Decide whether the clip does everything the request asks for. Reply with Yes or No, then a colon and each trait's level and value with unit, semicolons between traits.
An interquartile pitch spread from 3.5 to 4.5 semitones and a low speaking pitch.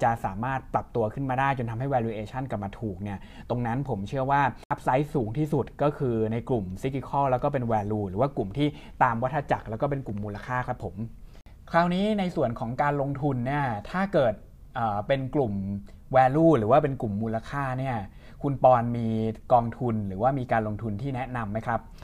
Yes: average, 4.0 semitones; low, 125 Hz